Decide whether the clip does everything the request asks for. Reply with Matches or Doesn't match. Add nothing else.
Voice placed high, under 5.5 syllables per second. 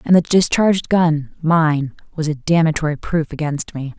Doesn't match